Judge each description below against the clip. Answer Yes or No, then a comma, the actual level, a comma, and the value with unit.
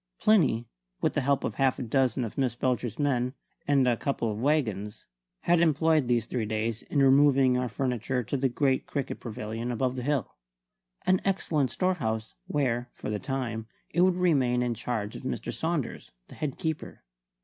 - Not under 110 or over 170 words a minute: No, average, 180 wpm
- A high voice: No, low, 130 Hz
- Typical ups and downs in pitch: Yes, average, 3.5 semitones